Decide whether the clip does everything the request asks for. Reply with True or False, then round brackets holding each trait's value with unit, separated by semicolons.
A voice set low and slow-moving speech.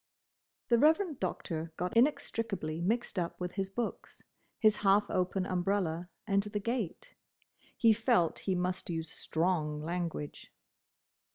False (190 Hz; 125 wpm)